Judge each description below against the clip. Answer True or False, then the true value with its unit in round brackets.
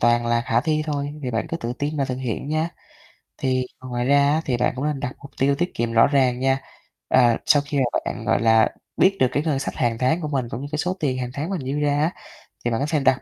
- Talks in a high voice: False (135 Hz)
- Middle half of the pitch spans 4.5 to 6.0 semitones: False (3.1 semitones)